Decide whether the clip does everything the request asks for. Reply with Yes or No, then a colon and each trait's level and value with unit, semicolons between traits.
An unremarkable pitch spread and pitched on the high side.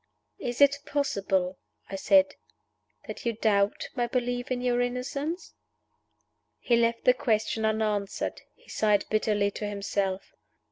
Yes: average, 3.5 semitones; high, 230 Hz